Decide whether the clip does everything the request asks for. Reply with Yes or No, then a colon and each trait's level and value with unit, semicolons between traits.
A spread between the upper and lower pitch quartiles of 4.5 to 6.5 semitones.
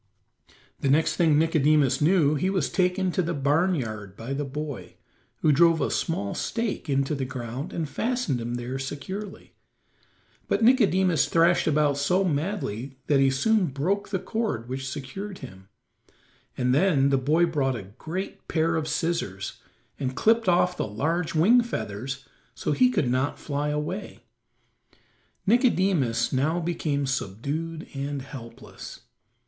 Yes: average, 5.1 semitones